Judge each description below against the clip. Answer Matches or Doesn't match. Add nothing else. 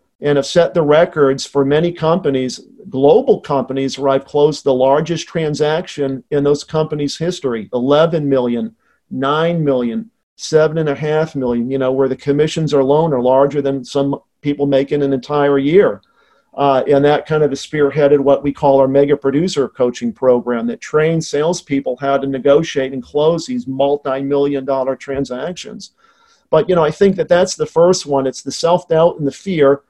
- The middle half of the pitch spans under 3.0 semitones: Matches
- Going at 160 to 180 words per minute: Matches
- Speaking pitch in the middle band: Matches